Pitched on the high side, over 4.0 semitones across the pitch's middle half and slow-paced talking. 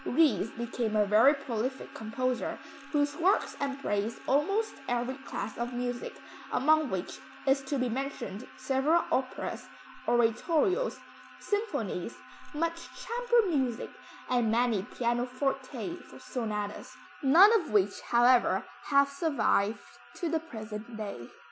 Yes: very high, 255 Hz; average, 4.7 semitones; slow, 115 wpm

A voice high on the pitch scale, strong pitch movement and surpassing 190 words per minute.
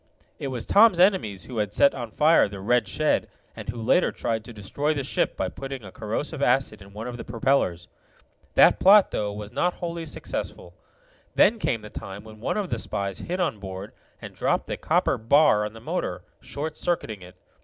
No: low, 115 Hz; wide, 6.4 semitones; fast, 205 wpm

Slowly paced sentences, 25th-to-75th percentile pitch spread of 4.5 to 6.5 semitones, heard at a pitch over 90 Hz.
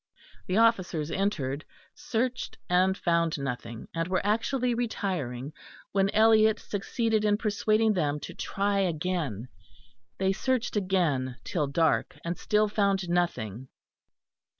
Yes: slow, 120 wpm; wide, 5.5 semitones; high, 190 Hz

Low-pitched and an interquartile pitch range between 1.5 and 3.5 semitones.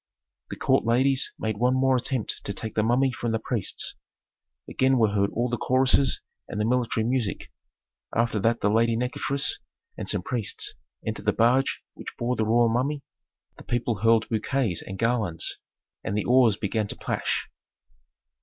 Yes: low, 120 Hz; average, 2.7 semitones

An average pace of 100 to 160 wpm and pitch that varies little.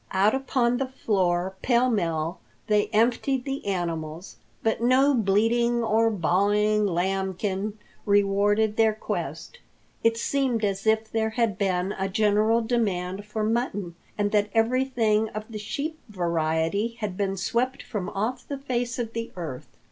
No: average, 145 wpm; average, 3.5 semitones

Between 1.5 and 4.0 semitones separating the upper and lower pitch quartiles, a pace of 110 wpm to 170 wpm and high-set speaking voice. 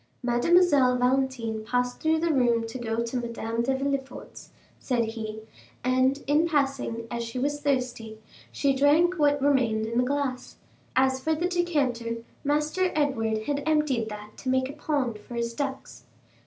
Yes: average, 3.7 semitones; average, 160 wpm; very high, 260 Hz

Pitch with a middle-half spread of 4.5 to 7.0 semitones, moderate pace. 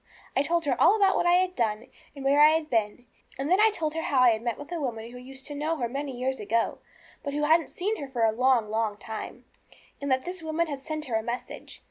No: average, 5.0 semitones; fast, 265 wpm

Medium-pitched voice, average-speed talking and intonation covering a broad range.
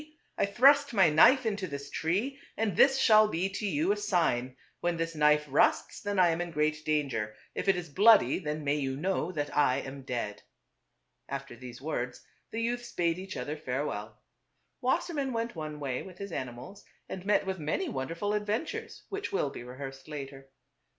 Yes: medium, 165 Hz; average, 185 wpm; wide, 6.7 semitones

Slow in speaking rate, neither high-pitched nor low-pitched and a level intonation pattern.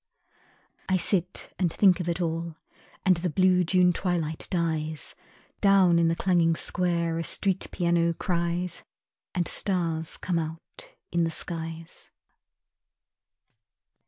Yes: slow, 125 wpm; medium, 170 Hz; narrow, 1.6 semitones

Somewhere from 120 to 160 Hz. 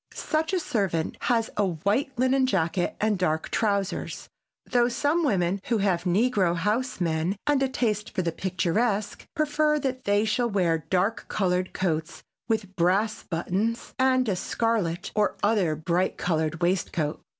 No: high, 200 Hz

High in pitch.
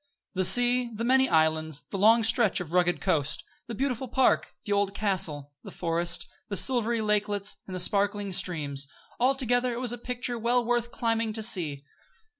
Yes: high, 210 Hz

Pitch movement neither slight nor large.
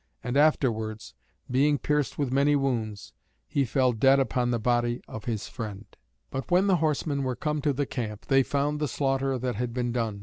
Yes: average, 3.3 semitones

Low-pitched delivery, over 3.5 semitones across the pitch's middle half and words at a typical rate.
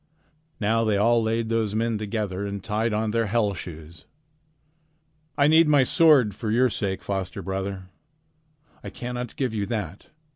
No: low, 110 Hz; average, 2.8 semitones; average, 155 wpm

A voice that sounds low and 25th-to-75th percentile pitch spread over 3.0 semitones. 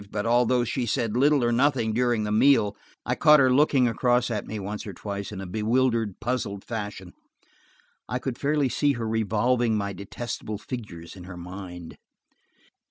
Yes: low, 115 Hz; average, 3.6 semitones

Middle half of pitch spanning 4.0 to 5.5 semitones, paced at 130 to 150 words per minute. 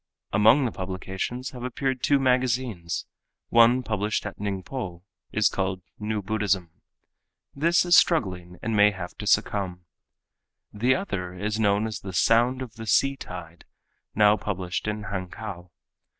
Yes: average, 4.6 semitones; average, 140 wpm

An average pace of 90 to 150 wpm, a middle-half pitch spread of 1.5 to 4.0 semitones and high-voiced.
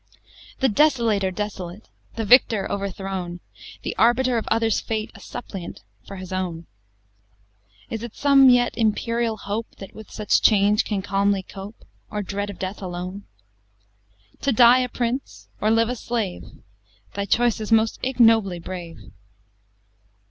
Yes: average, 145 wpm; average, 3.3 semitones; high, 210 Hz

